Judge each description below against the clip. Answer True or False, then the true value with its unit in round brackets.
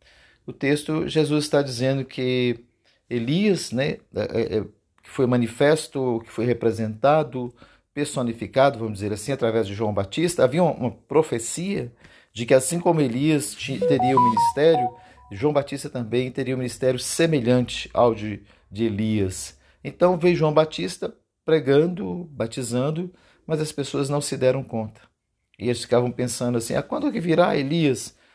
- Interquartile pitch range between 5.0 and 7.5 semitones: False (4.5 semitones)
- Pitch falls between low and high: False (130 Hz)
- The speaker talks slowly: False (155 wpm)